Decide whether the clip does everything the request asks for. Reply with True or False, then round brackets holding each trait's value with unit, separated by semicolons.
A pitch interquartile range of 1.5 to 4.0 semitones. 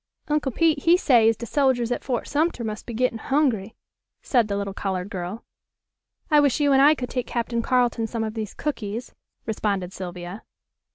False (4.4 semitones)